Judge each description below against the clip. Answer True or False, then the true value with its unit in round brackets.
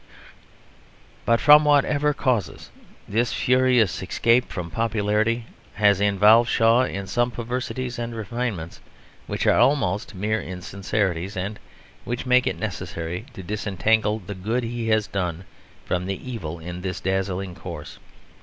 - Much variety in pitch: False (4.2 semitones)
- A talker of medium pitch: False (105 Hz)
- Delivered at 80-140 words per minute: True (135 wpm)